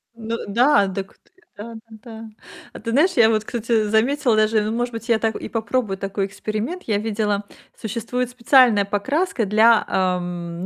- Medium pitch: No, high, 220 Hz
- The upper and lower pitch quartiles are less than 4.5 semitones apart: Yes, narrow, 2.4 semitones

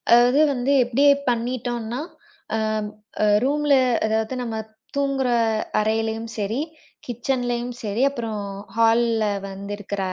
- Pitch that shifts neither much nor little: No, narrow, 2.2 semitones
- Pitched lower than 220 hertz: No, high, 235 Hz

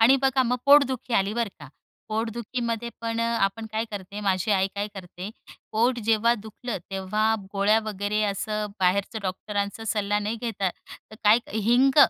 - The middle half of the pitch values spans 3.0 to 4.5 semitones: No, narrow, 2.5 semitones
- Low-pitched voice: No, high, 215 Hz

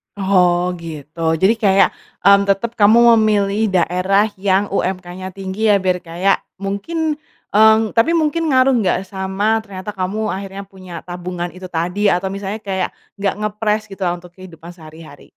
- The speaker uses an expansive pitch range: No, average, 2.7 semitones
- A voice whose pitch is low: No, high, 195 Hz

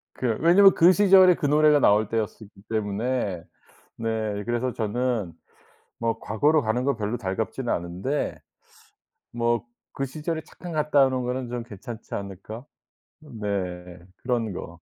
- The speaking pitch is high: No, low, 120 Hz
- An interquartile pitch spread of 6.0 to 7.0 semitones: No, average, 5.1 semitones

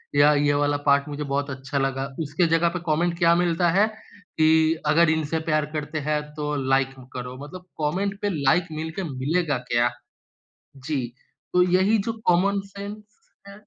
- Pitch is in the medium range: Yes, medium, 155 Hz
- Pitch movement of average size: Yes, average, 3.7 semitones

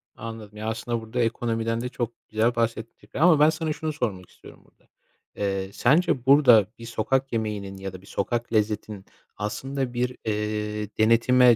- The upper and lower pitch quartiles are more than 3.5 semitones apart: No, average, 2.8 semitones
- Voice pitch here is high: No, low, 115 Hz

